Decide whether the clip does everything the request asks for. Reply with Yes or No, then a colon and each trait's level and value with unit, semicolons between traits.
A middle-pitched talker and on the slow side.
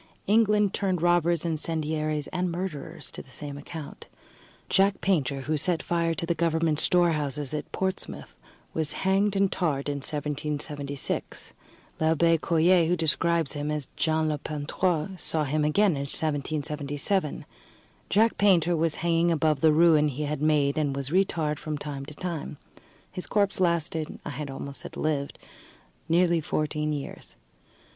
No: medium, 155 Hz; average, 150 wpm